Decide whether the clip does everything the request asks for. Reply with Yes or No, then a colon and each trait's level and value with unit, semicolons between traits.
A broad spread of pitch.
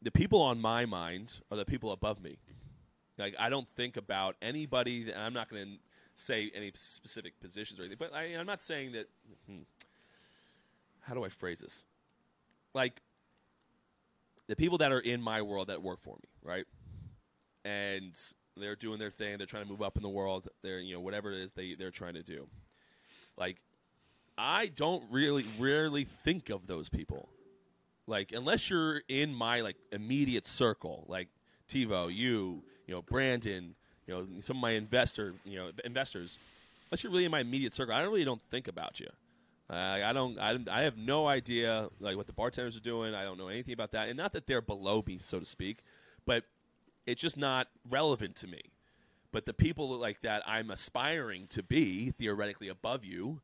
No: average, 4.4 semitones